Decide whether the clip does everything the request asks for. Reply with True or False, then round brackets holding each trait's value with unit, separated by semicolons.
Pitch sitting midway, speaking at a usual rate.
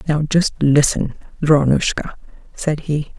False (150 Hz; 115 wpm)